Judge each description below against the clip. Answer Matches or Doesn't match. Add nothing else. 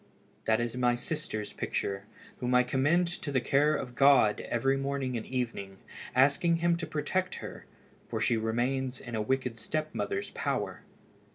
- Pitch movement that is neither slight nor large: Matches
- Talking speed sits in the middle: Matches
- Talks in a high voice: Doesn't match